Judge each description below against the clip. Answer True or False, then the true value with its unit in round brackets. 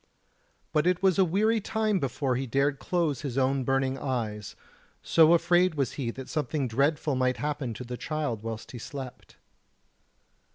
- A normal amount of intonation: True (4.3 semitones)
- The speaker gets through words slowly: False (165 wpm)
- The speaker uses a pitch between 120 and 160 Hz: True (140 Hz)